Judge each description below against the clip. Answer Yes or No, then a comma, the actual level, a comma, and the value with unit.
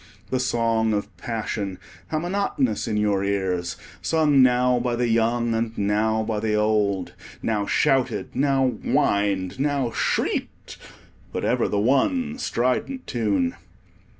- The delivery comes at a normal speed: No, slow, 130 wpm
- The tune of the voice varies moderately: Yes, average, 3.8 semitones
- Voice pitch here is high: No, low, 115 Hz